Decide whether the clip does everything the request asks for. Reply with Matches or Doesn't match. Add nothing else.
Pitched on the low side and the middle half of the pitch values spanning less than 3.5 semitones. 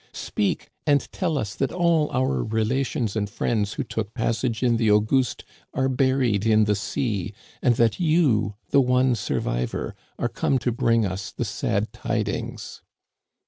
Doesn't match